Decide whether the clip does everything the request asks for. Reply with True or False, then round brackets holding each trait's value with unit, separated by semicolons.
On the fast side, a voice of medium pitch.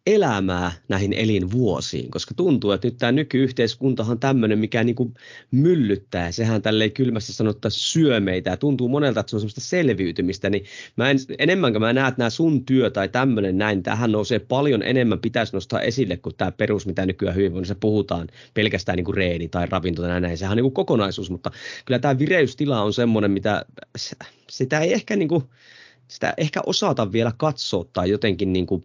False (180 wpm; 110 Hz)